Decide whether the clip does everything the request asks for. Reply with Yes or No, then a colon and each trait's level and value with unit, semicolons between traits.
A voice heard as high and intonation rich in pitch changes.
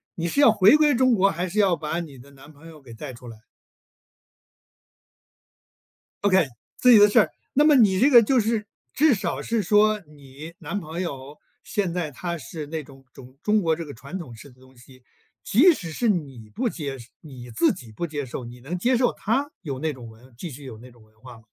No: medium, 160 Hz; wide, 7.9 semitones